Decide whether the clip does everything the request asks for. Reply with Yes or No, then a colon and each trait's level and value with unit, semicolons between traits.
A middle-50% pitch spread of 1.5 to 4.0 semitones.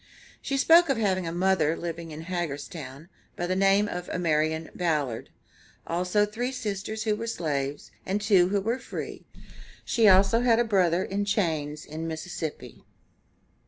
No: average, 4.5 semitones